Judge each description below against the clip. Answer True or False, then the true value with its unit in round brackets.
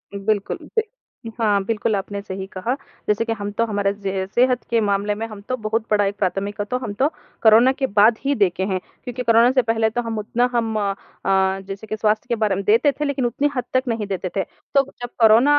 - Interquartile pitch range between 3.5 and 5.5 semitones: False (3.1 semitones)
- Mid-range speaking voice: False (220 Hz)